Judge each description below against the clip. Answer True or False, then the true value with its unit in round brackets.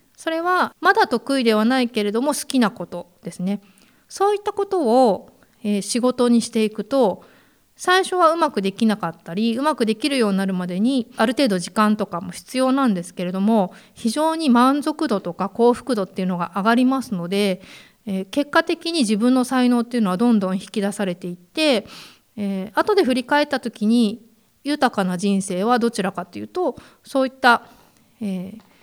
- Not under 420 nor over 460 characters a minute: False (350 characters per minute)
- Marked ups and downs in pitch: False (5.0 semitones)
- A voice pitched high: True (230 Hz)